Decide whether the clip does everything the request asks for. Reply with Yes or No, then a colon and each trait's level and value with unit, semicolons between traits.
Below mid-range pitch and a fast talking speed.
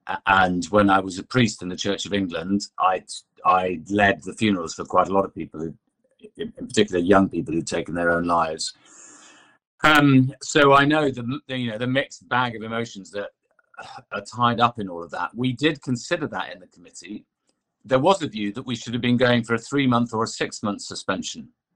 Yes: low, 115 Hz; fast, 215 wpm